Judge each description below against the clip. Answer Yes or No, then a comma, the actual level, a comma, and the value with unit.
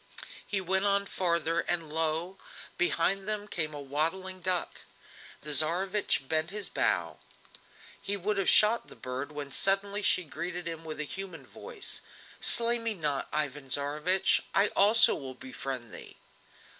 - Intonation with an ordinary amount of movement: Yes, average, 4.6 semitones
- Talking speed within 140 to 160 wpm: Yes, average, 150 wpm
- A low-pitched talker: No, medium, 175 Hz